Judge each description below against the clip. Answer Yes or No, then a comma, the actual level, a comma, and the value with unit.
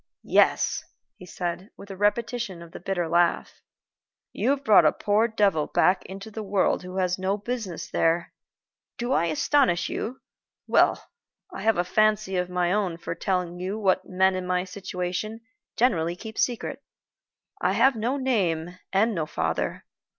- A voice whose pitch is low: No, high, 190 Hz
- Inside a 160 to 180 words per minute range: Yes, average, 165 wpm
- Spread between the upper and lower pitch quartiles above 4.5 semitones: No, average, 3.5 semitones